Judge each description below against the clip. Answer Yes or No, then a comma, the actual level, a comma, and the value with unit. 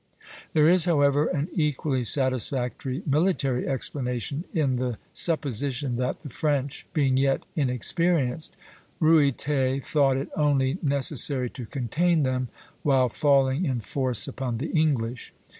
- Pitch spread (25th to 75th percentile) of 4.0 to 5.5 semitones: No, average, 2.8 semitones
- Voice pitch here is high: No, low, 135 Hz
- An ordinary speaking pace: No, slow, 125 wpm